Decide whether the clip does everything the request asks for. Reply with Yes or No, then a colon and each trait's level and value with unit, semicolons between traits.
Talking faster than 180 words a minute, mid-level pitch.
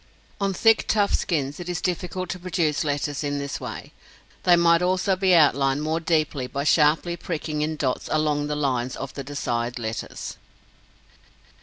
No: average, 165 wpm; medium, 155 Hz